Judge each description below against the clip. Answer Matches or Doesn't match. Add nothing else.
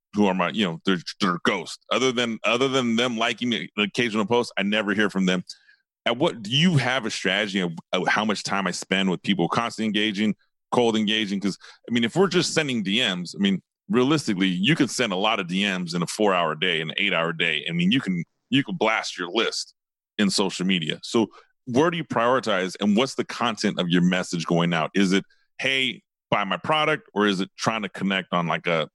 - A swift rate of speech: Matches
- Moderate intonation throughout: Doesn't match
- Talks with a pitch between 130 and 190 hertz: Doesn't match